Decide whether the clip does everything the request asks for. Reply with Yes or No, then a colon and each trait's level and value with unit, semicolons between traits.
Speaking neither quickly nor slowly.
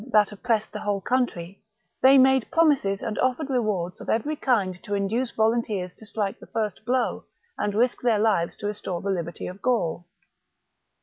Yes: average, 175 wpm